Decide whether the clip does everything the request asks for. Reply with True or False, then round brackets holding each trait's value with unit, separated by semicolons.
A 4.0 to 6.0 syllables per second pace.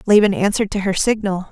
False (6.5 syllables/s)